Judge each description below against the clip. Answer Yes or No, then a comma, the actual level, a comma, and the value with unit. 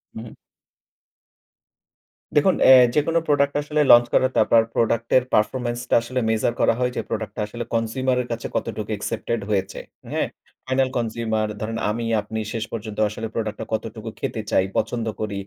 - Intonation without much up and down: Yes, narrow, 2.3 semitones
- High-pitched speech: No, low, 115 Hz